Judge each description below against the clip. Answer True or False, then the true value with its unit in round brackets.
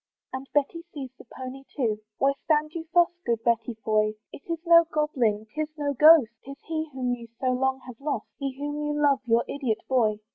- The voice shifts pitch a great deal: False (4.0 semitones)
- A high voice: True (270 Hz)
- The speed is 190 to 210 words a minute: True (205 wpm)